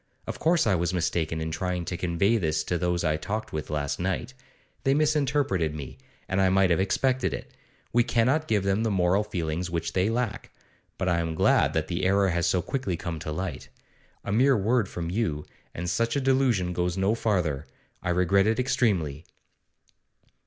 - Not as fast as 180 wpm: No, average, 190 wpm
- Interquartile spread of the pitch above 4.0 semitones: Yes, average, 4.9 semitones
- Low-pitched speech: Yes, very low, 95 Hz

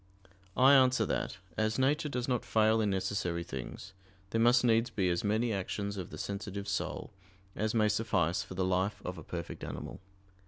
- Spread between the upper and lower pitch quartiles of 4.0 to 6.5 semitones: No, average, 3.5 semitones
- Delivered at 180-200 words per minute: Yes, average, 185 wpm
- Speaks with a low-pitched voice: Yes, low, 105 Hz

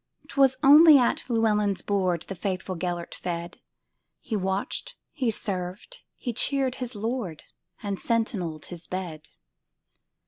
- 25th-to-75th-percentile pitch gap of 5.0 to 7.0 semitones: Yes, average, 5.3 semitones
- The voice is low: No, high, 200 Hz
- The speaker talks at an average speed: No, slow, 110 wpm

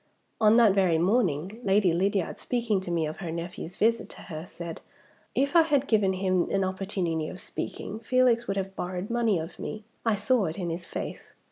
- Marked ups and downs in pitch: No, average, 4.3 semitones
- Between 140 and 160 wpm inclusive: No, average, 200 wpm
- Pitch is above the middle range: Yes, high, 195 Hz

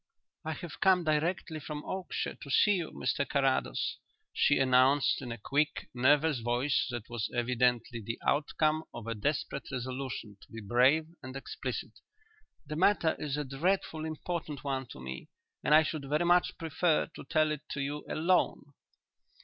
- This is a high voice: No, medium, 145 Hz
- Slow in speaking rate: No, average, 165 wpm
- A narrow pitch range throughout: No, average, 3.7 semitones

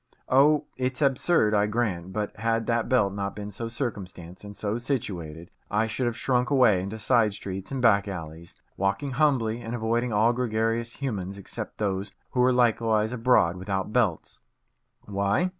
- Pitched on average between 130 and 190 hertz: No, low, 110 Hz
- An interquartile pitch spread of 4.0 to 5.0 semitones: No, average, 3.6 semitones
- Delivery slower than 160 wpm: No, average, 165 wpm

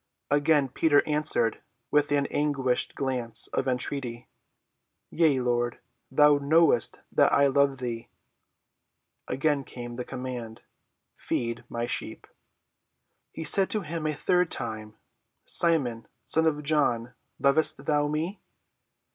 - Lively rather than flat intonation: No, average, 3.9 semitones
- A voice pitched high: No, medium, 140 Hz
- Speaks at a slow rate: Yes, slow, 120 wpm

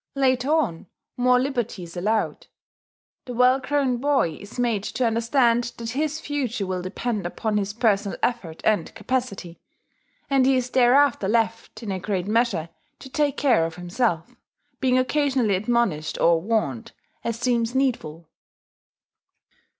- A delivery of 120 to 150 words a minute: Yes, average, 140 wpm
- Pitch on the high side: Yes, high, 235 Hz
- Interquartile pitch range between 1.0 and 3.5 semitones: No, average, 4.5 semitones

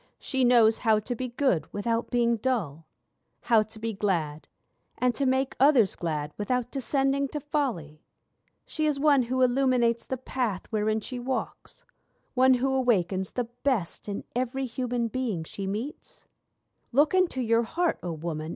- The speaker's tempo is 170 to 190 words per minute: No, average, 160 wpm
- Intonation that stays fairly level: No, average, 4.0 semitones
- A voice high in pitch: Yes, high, 240 Hz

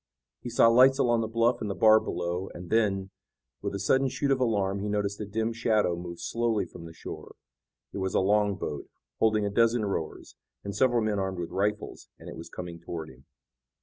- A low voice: Yes, low, 105 Hz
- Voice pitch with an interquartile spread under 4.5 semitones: Yes, average, 3.7 semitones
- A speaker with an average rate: No, fast, 215 wpm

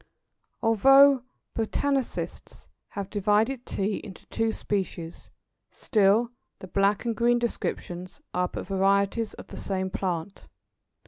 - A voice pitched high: Yes, high, 205 Hz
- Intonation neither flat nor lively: Yes, average, 3.5 semitones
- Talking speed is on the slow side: Yes, slow, 115 wpm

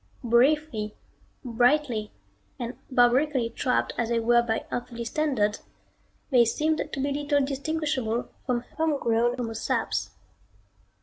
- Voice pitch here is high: Yes, high, 245 Hz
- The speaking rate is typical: No, slow, 115 wpm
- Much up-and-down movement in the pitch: No, average, 3.7 semitones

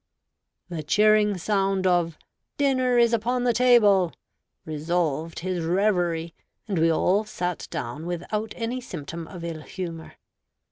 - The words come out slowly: Yes, slow, 130 wpm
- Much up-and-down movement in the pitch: No, average, 4.5 semitones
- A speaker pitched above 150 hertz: Yes, medium, 185 Hz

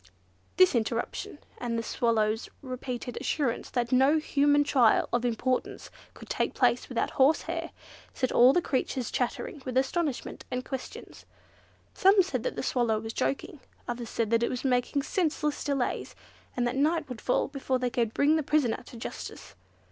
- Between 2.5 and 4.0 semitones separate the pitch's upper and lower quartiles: Yes, average, 3.4 semitones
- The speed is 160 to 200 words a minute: Yes, average, 165 wpm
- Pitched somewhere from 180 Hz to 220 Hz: No, very high, 255 Hz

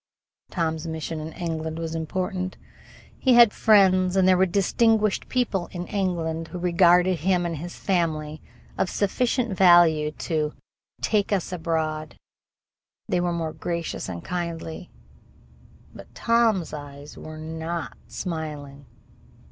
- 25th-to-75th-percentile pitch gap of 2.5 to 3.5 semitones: Yes, average, 2.8 semitones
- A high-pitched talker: No, medium, 170 Hz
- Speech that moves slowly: Yes, slow, 125 wpm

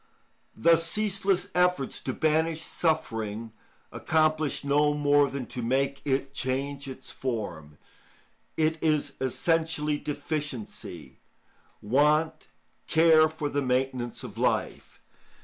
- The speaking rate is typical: No, slow, 105 wpm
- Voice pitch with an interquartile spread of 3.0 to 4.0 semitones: Yes, average, 3.4 semitones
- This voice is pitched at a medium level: Yes, medium, 145 Hz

